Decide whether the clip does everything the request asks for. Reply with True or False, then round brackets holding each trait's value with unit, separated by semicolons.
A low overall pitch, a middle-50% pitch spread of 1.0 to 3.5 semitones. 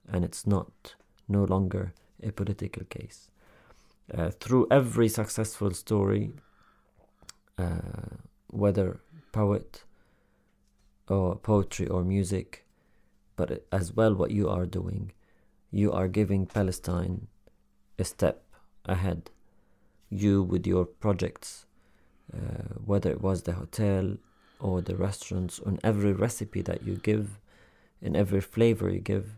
True (100 Hz; 2.5 semitones)